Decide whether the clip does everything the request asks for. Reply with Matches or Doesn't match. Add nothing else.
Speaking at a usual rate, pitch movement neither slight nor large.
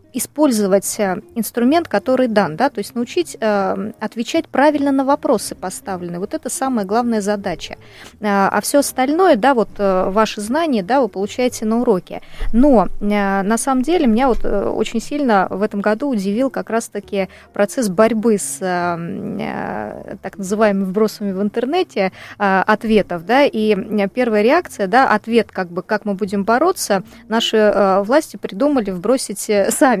Matches